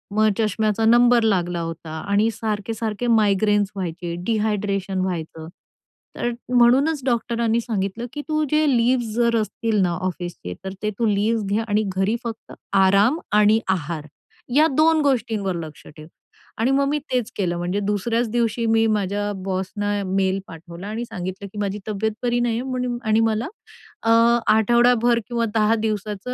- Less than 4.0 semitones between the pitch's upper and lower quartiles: Yes, average, 3.4 semitones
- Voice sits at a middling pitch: No, high, 215 Hz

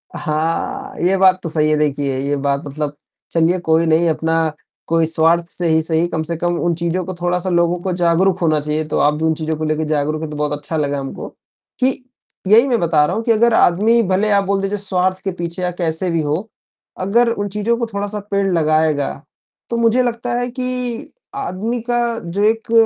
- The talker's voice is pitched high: No, medium, 170 Hz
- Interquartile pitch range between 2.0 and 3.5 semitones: No, average, 4.1 semitones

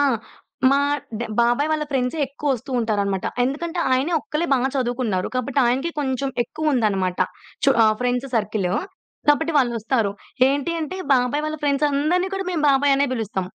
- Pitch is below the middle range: No, very high, 265 Hz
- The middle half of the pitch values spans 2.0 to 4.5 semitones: Yes, average, 4.1 semitones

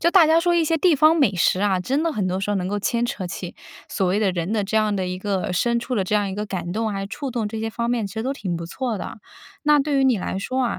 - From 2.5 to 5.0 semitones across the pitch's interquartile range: No, wide, 5.5 semitones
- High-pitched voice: Yes, high, 215 Hz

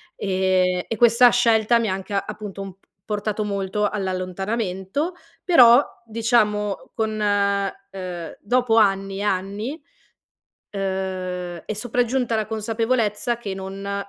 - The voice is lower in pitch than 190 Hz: No, high, 205 Hz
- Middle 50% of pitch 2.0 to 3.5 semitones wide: Yes, average, 2.9 semitones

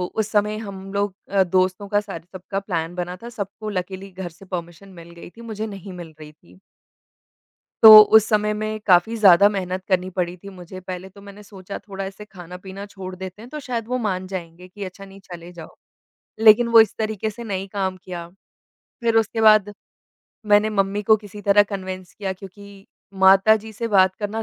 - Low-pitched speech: No, high, 195 Hz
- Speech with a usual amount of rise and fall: No, narrow, 2.3 semitones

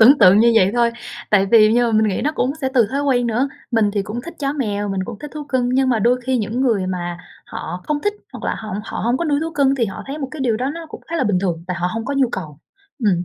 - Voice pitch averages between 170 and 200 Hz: No, high, 235 Hz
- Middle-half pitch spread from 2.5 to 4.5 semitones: No, average, 5.0 semitones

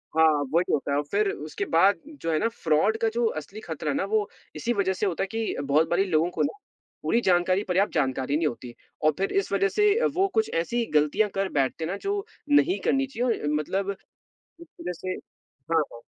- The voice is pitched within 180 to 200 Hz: Yes, high, 190 Hz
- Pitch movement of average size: No, wide, 6.4 semitones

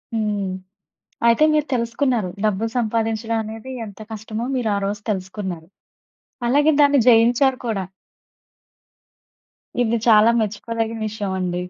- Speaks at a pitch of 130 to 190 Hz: No, high, 220 Hz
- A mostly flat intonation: Yes, narrow, 2.2 semitones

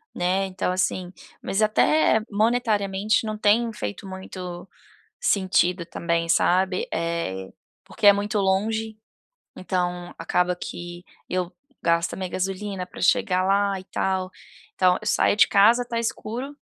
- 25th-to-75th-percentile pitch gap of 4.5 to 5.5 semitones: No, average, 2.9 semitones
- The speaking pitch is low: No, high, 190 Hz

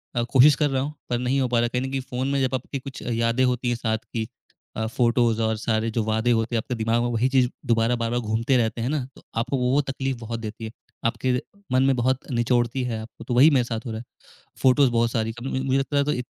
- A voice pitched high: No, low, 120 Hz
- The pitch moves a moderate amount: No, narrow, 2.3 semitones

